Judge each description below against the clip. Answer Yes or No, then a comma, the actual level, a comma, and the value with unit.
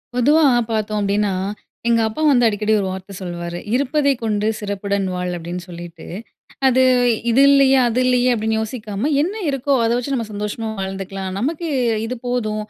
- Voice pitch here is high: Yes, high, 215 Hz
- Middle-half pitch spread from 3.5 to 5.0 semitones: Yes, average, 4.4 semitones